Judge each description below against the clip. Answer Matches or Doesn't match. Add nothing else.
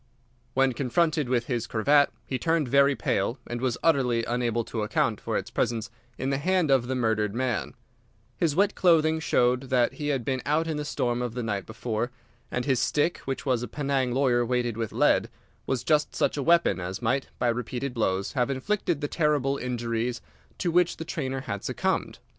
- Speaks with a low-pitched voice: Matches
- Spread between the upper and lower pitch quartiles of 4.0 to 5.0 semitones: Doesn't match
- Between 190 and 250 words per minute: Matches